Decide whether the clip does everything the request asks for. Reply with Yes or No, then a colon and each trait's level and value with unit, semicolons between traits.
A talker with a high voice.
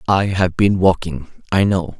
No: very low, 90 Hz